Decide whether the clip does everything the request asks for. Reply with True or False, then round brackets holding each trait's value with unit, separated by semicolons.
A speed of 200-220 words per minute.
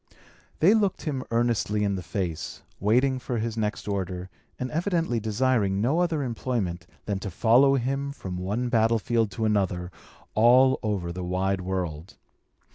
False (150 wpm)